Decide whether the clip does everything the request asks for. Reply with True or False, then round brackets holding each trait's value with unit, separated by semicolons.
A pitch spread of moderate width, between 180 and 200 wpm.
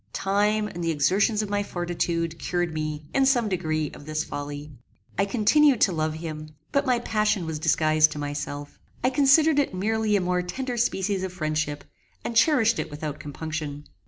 False (5.8 semitones; 185 wpm)